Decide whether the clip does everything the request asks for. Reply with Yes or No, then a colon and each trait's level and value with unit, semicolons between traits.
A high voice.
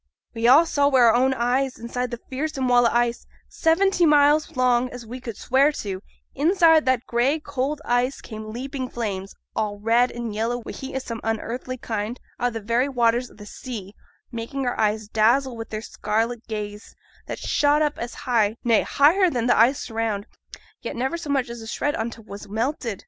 Yes: high, 245 Hz